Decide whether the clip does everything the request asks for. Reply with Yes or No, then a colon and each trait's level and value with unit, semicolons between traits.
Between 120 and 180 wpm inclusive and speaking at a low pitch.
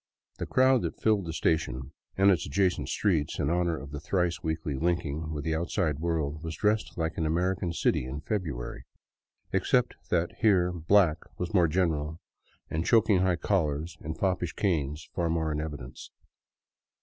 Yes: average, 165 wpm; very low, 85 Hz